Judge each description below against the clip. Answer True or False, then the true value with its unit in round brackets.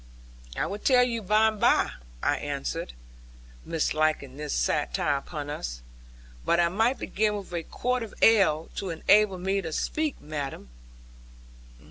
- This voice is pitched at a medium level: True (180 Hz)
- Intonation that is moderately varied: False (6.0 semitones)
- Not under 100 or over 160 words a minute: True (145 wpm)